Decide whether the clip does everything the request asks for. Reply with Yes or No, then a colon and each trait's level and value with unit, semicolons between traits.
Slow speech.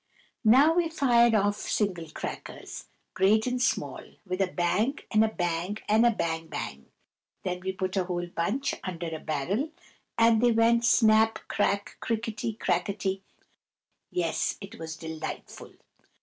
No: average, 145 wpm